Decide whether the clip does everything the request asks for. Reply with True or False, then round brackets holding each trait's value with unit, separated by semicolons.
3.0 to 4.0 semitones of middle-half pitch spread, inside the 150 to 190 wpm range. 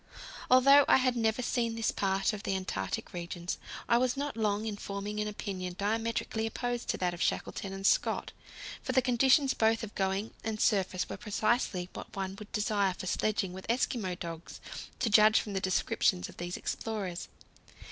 True (3.3 semitones; 180 wpm)